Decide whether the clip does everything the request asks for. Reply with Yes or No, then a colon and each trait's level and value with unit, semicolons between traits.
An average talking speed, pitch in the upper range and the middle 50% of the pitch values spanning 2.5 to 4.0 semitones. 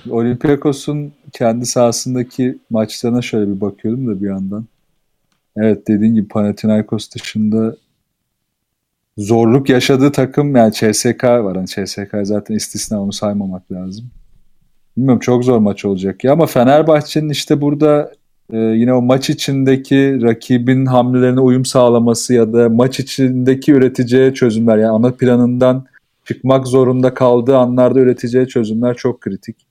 No: average, 130 wpm; low, 125 Hz; average, 3.0 semitones